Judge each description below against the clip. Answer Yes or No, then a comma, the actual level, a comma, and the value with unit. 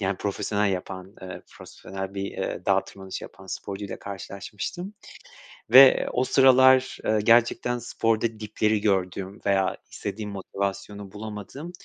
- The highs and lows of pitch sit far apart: No, average, 3.0 semitones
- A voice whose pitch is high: No, low, 105 Hz